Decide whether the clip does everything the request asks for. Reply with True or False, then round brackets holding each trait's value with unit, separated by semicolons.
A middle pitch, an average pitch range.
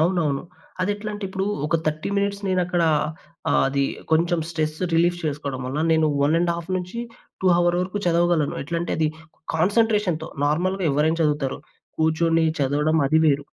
True (165 Hz; 3.0 semitones)